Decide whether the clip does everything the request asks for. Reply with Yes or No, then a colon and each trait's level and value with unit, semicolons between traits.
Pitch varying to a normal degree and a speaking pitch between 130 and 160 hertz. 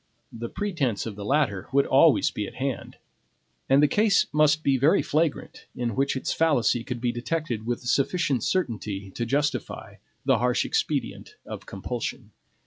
Yes: average, 4.5 semitones; low, 135 Hz